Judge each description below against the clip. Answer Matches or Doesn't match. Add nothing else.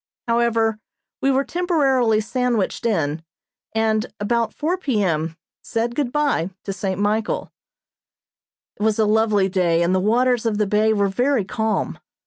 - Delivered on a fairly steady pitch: Doesn't match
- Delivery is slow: Doesn't match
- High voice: Matches